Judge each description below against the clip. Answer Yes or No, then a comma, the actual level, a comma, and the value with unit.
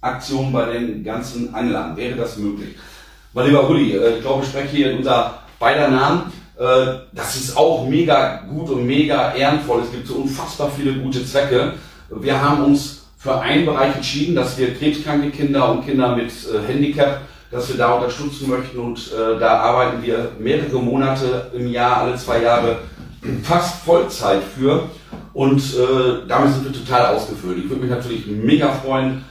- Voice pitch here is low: Yes, low, 130 Hz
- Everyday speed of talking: Yes, average, 165 wpm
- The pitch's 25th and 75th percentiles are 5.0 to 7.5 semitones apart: No, average, 2.7 semitones